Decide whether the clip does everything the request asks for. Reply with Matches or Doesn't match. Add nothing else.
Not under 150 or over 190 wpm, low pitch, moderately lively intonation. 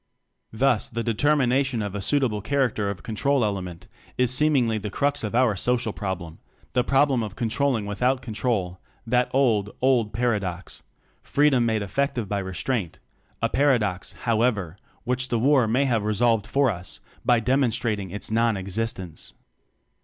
Matches